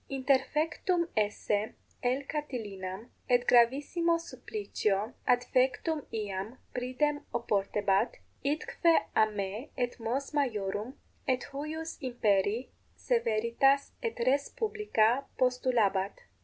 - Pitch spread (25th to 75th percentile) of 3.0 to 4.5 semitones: No, average, 4.9 semitones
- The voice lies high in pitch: Yes, very high, 250 Hz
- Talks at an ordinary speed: No, slow, 90 wpm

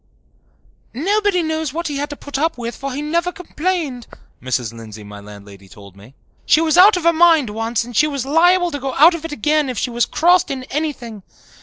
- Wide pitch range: Yes, wide, 6.3 semitones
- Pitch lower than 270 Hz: No, very high, 285 Hz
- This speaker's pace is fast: Yes, fast, 215 wpm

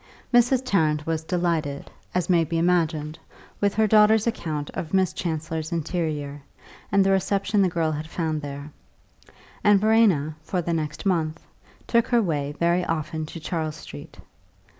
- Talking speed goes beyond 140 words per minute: Yes, average, 160 wpm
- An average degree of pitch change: Yes, average, 3.8 semitones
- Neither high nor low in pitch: Yes, medium, 165 Hz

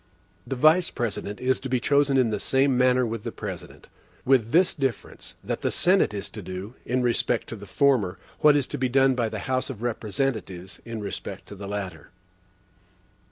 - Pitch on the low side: Yes, low, 120 Hz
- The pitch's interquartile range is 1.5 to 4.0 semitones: No, average, 4.5 semitones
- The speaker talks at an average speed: Yes, average, 195 wpm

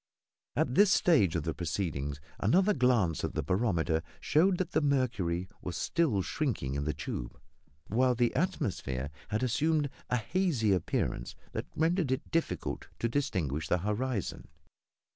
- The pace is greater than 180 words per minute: No, average, 145 wpm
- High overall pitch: No, low, 110 Hz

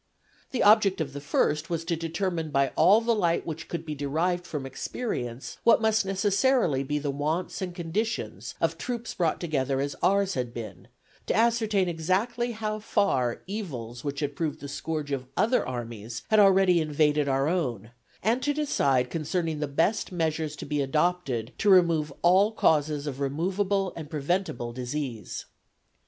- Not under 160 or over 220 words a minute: Yes, average, 165 wpm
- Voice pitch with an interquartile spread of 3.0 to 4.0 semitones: No, wide, 5.6 semitones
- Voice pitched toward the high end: No, medium, 160 Hz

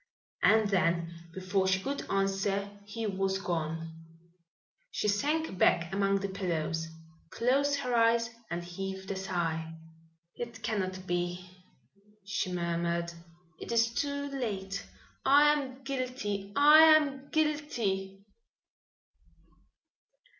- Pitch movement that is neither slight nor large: No, wide, 5.7 semitones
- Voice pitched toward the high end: Yes, high, 195 Hz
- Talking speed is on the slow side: Yes, slow, 110 wpm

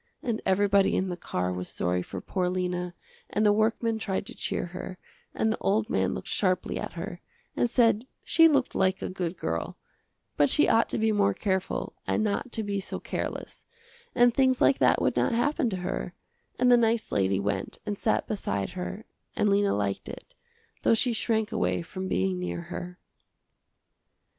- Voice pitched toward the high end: Yes, high, 200 Hz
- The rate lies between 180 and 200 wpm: Yes, average, 185 wpm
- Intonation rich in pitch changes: No, average, 3.8 semitones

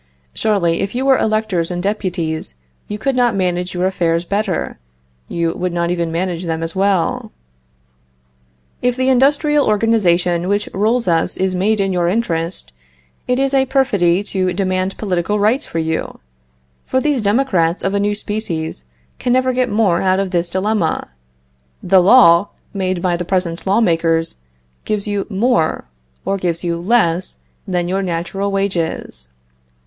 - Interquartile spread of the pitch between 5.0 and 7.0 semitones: No, average, 3.9 semitones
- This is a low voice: No, high, 190 Hz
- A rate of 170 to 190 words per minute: No, average, 155 wpm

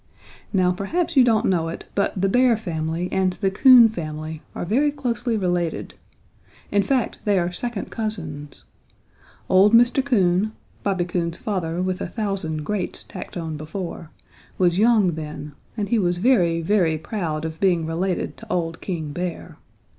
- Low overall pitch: No, medium, 185 Hz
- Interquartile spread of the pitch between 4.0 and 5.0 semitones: Yes, average, 4.6 semitones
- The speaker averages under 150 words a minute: No, average, 160 wpm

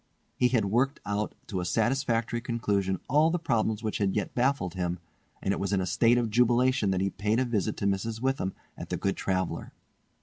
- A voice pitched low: Yes, low, 110 Hz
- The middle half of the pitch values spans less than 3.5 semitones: No, average, 4.0 semitones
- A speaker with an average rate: No, fast, 215 wpm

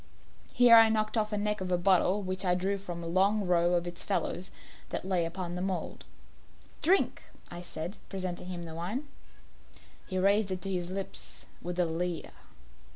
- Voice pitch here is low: No, medium, 185 Hz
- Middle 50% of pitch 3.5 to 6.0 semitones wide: No, narrow, 2.4 semitones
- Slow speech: No, average, 185 wpm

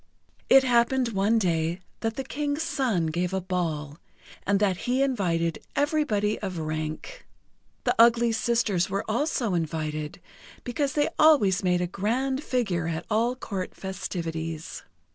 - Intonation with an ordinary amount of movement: No, wide, 6.6 semitones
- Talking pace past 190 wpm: No, average, 140 wpm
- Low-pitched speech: No, high, 200 Hz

